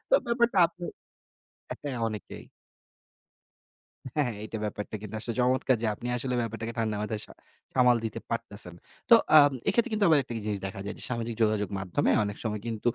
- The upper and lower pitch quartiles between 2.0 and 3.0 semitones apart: No, average, 3.5 semitones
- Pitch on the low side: Yes, low, 115 Hz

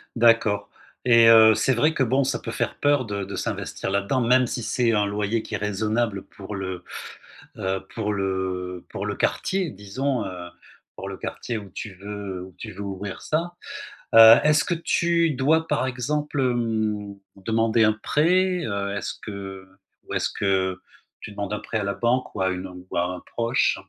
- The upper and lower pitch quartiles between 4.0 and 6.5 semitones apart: Yes, average, 4.6 semitones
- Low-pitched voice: Yes, low, 110 Hz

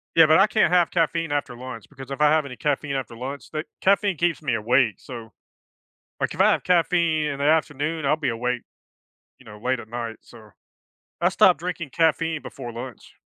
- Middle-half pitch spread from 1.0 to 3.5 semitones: No, average, 4.6 semitones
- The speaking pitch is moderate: Yes, medium, 145 Hz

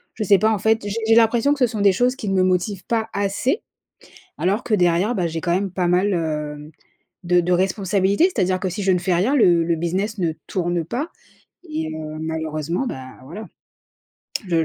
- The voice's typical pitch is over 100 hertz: Yes, medium, 185 Hz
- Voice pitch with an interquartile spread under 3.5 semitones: No, average, 4.1 semitones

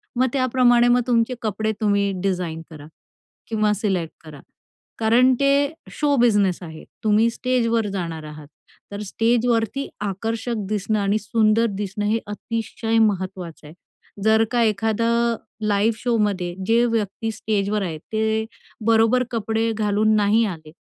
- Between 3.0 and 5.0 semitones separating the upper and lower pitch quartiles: No, narrow, 2.5 semitones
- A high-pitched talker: Yes, high, 215 Hz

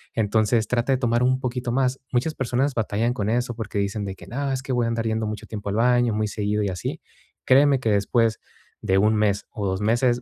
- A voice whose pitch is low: Yes, low, 115 Hz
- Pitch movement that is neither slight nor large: Yes, average, 3.0 semitones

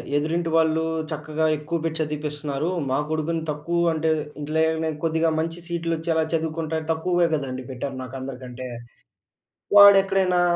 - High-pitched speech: No, medium, 160 Hz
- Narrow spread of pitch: Yes, narrow, 1.9 semitones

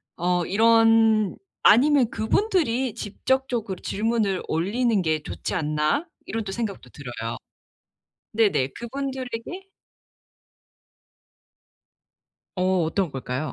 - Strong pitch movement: No, average, 5.0 semitones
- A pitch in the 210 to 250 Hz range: Yes, high, 220 Hz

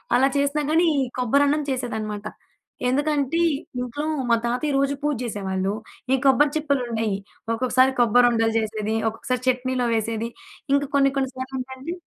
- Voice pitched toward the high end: Yes, very high, 255 Hz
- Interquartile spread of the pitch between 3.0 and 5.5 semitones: Yes, average, 3.7 semitones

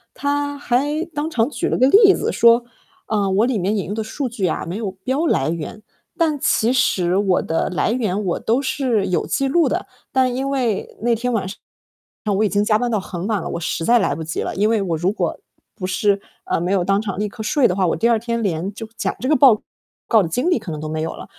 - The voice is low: No, high, 220 Hz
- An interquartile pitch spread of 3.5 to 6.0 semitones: Yes, average, 5.1 semitones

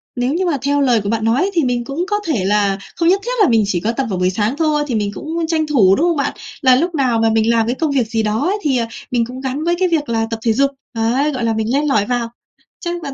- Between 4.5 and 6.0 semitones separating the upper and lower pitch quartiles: Yes, average, 5.2 semitones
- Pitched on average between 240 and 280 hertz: Yes, very high, 255 Hz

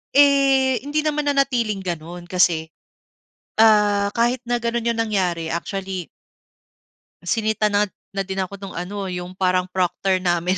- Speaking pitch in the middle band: No, high, 200 Hz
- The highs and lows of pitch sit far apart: No, average, 4.5 semitones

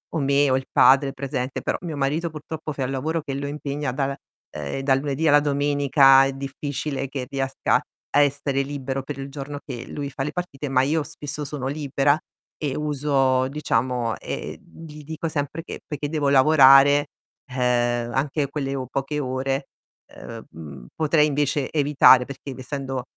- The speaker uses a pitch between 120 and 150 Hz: Yes, medium, 140 Hz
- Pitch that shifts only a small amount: Yes, narrow, 1.7 semitones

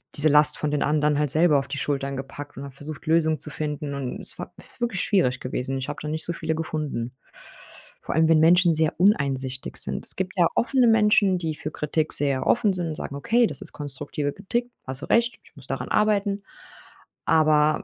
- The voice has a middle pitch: Yes, medium, 155 Hz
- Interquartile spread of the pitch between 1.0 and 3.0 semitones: No, average, 4.0 semitones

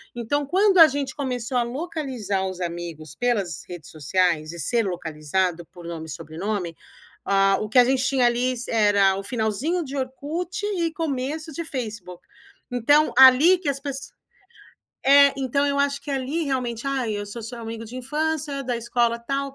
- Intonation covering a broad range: Yes, wide, 6.1 semitones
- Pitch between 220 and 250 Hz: Yes, high, 245 Hz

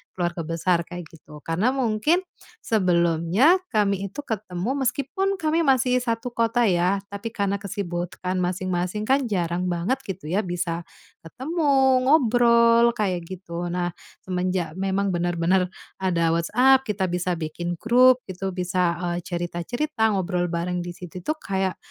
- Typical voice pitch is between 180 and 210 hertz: Yes, high, 190 Hz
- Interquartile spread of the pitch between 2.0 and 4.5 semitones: No, average, 5.2 semitones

